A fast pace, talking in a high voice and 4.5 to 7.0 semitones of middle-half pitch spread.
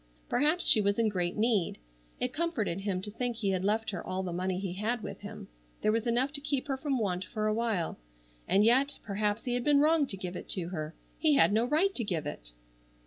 Yes: fast, 240 wpm; high, 215 Hz; average, 5.1 semitones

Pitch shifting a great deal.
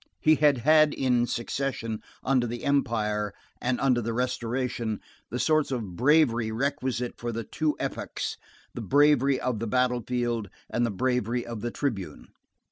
No: average, 2.9 semitones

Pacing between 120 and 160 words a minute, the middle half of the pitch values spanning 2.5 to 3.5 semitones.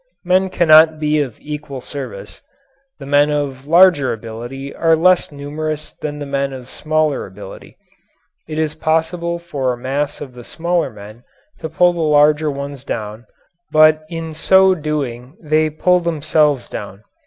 Yes: average, 155 wpm; average, 2.9 semitones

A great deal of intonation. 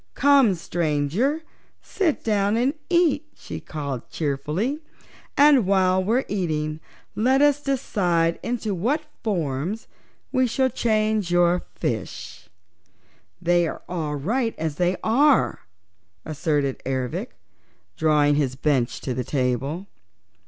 Yes: wide, 8.2 semitones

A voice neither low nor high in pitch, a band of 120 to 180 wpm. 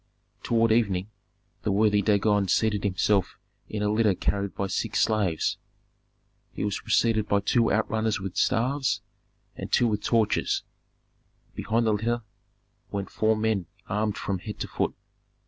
No: low, 105 Hz; average, 145 wpm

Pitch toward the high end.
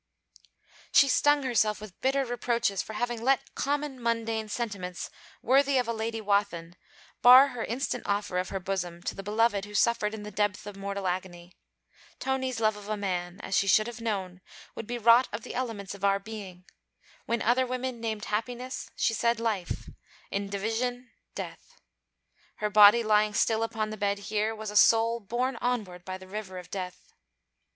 Yes: high, 215 Hz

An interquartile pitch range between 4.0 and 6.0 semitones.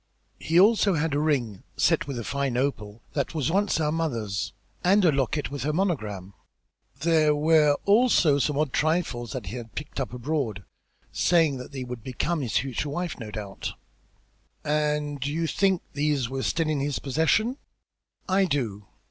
Yes: average, 4.5 semitones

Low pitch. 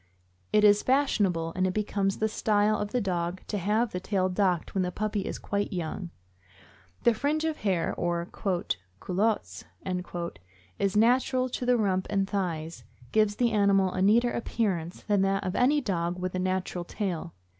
No: high, 195 Hz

